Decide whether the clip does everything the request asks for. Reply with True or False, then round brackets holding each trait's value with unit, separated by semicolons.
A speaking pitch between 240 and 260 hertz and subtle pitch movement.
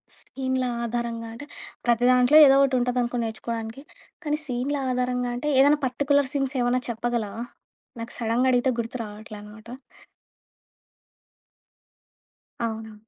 True (245 Hz; 2.2 semitones)